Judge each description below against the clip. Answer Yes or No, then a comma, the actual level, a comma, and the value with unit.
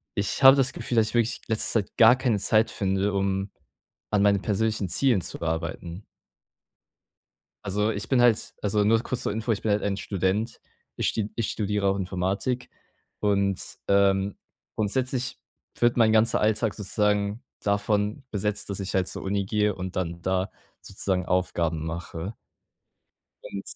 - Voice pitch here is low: Yes, low, 100 Hz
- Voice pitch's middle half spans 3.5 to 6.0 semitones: No, narrow, 2.4 semitones